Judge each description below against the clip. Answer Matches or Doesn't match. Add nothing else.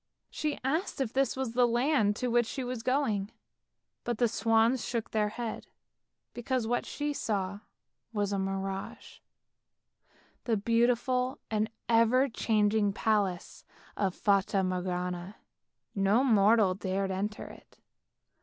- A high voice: Matches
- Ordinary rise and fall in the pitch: Matches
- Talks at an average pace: Doesn't match